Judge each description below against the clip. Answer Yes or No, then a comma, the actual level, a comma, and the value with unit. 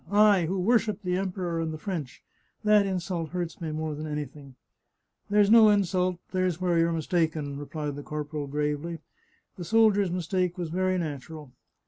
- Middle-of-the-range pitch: Yes, medium, 170 Hz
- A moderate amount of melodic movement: Yes, average, 3.6 semitones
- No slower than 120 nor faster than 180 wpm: No, average, 190 wpm